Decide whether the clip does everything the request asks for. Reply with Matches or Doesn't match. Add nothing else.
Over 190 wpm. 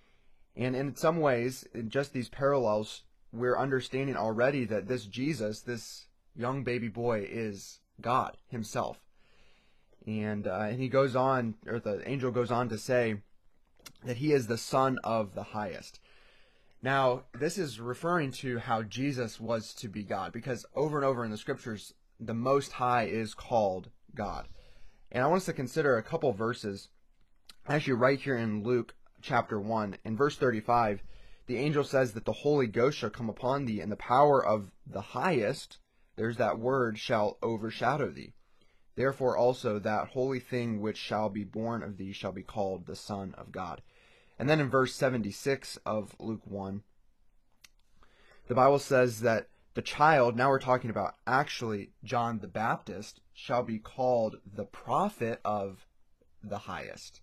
Doesn't match